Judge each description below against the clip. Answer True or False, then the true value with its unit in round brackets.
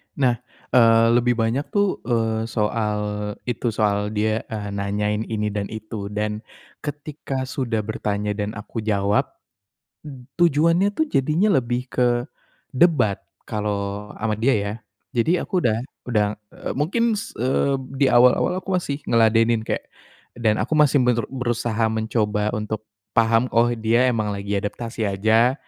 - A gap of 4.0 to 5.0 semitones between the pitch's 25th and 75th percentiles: False (3.6 semitones)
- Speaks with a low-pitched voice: True (115 Hz)